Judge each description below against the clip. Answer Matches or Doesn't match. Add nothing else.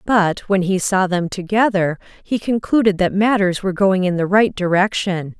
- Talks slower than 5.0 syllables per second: Matches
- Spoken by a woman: Matches